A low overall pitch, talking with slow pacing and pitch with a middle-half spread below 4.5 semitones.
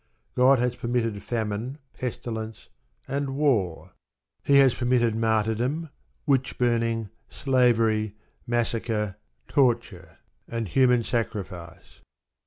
Yes: low, 120 Hz; slow, 90 wpm; narrow, 2.5 semitones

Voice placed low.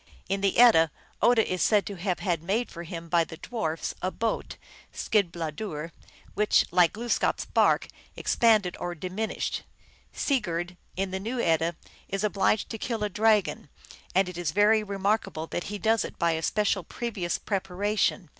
No: high, 195 Hz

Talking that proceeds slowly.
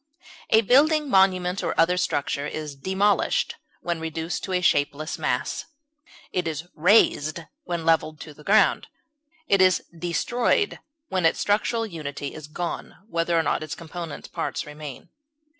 No: average, 145 wpm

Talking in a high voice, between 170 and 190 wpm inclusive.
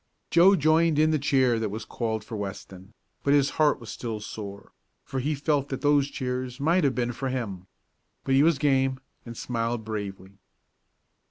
No: low, 130 Hz; average, 180 wpm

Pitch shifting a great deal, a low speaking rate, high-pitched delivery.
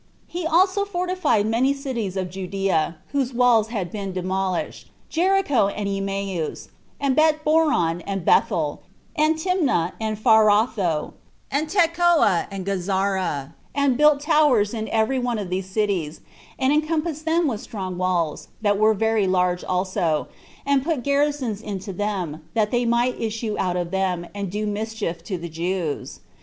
No: wide, 7.1 semitones; average, 150 wpm; high, 210 Hz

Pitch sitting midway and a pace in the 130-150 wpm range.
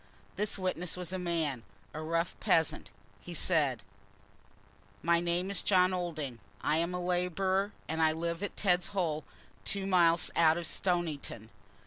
Yes: medium, 175 Hz; average, 145 wpm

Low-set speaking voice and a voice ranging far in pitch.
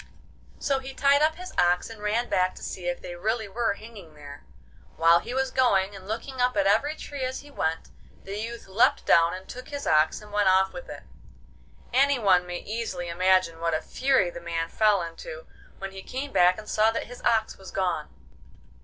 No: high, 205 Hz; wide, 5.8 semitones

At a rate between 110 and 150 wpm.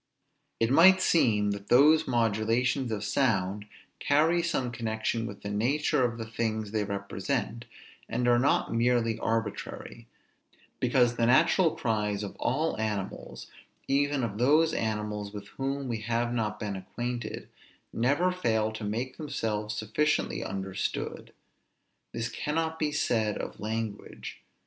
Yes: slow, 135 wpm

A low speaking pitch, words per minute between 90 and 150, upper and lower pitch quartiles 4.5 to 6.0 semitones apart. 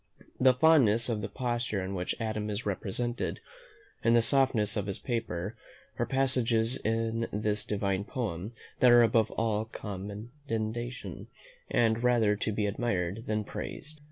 No: low, 110 Hz; average, 145 wpm; narrow, 2.6 semitones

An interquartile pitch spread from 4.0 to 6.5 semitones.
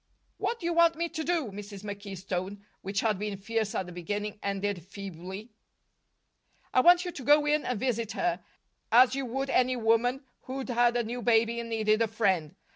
Yes: average, 4.5 semitones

